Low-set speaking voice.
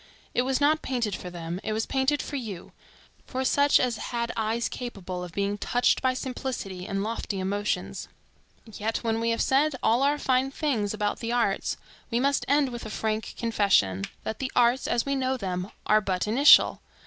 No: high, 230 Hz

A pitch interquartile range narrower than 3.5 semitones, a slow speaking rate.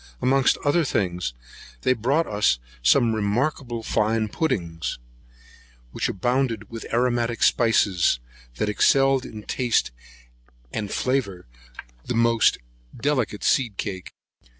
No: average, 3.8 semitones; slow, 110 wpm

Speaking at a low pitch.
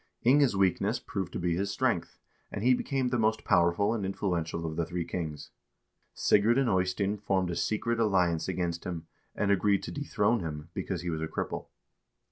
Yes: very low, 95 Hz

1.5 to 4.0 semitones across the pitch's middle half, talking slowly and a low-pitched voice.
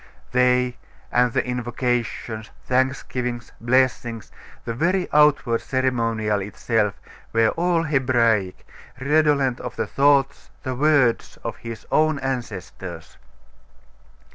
Yes: average, 2.9 semitones; slow, 100 wpm; low, 125 Hz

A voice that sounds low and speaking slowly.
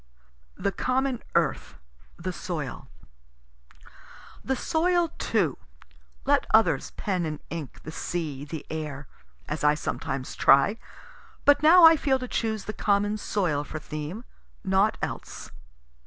No: high, 195 Hz; slow, 125 wpm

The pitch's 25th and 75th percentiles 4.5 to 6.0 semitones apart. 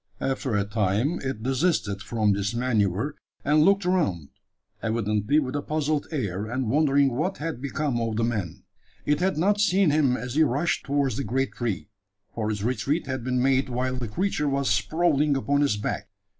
Yes: average, 5.3 semitones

